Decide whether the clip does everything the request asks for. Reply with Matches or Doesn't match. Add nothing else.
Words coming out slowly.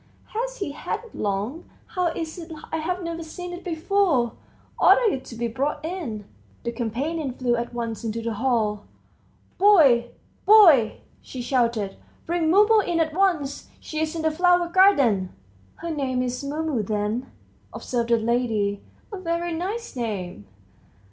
Doesn't match